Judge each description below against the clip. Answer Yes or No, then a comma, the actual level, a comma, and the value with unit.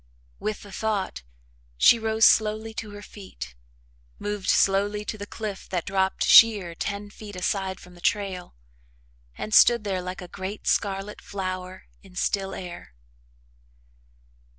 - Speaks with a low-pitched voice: No, high, 200 Hz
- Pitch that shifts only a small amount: Yes, narrow, 2.2 semitones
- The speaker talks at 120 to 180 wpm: Yes, average, 140 wpm